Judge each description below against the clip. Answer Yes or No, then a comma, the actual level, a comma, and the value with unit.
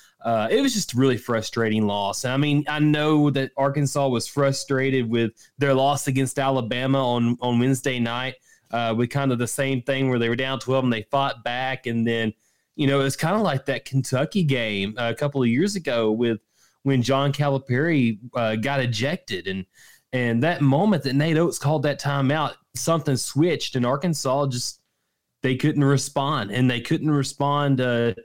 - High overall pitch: No, low, 135 Hz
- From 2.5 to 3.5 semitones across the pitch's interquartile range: Yes, average, 2.8 semitones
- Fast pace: No, average, 190 wpm